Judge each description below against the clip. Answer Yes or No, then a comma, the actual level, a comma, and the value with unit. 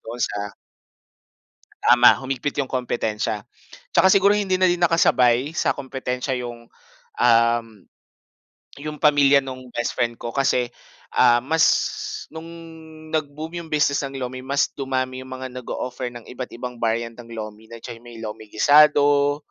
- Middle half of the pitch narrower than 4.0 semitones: Yes, average, 3.3 semitones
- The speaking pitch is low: Yes, low, 130 Hz